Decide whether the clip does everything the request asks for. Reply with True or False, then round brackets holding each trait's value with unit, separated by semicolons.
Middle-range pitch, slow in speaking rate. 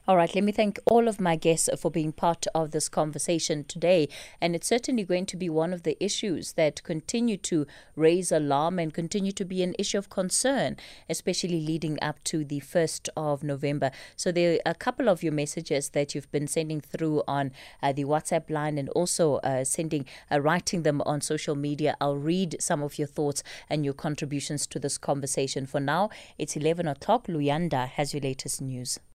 False (160 Hz; 200 wpm)